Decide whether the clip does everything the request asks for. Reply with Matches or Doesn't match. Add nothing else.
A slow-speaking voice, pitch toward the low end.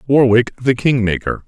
Matches